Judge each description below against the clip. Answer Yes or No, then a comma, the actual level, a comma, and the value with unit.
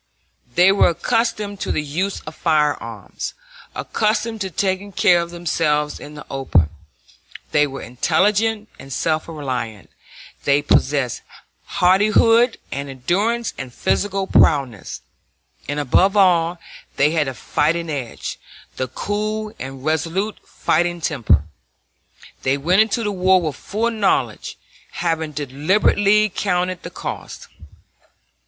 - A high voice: No, medium, 170 Hz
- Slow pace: Yes, slow, 120 wpm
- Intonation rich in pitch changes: Yes, wide, 5.8 semitones